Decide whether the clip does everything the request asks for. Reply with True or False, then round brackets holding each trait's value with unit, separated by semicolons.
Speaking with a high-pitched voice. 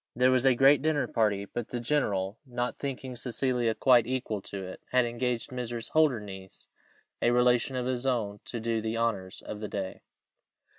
False (120 Hz)